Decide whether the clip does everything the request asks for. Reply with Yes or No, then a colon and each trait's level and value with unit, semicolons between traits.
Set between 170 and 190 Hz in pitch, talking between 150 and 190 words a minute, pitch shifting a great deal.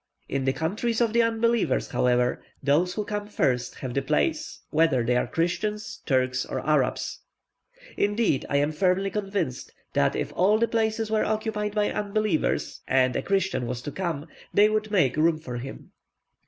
Yes: medium, 185 Hz; average, 170 wpm; wide, 7.8 semitones